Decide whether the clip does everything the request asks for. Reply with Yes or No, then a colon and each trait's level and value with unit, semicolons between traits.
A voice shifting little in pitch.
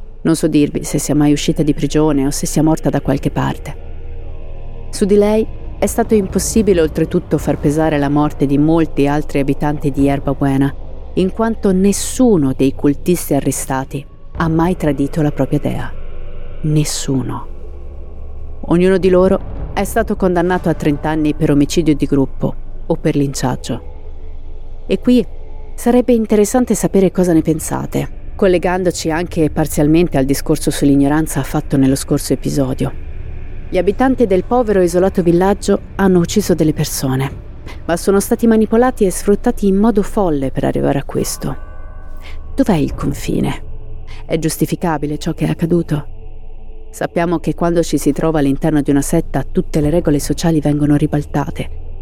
No: average, 4.8 semitones